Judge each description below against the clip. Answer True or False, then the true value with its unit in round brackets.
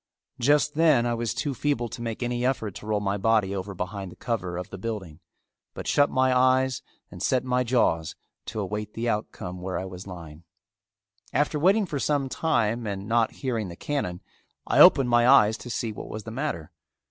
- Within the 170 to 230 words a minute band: True (200 wpm)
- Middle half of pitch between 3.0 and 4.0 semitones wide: False (4.9 semitones)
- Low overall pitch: True (115 Hz)